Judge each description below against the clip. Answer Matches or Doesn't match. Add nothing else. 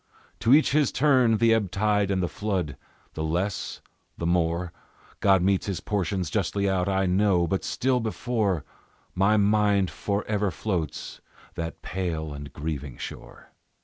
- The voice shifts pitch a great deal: Doesn't match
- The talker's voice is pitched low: Matches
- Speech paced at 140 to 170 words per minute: Matches